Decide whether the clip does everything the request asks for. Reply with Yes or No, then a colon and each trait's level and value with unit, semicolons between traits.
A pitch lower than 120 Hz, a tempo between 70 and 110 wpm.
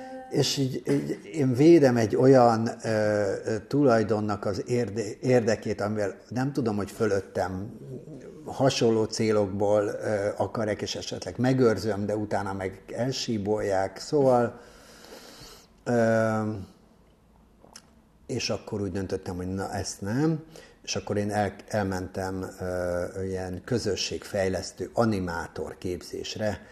Yes: low, 110 Hz; slow, 105 wpm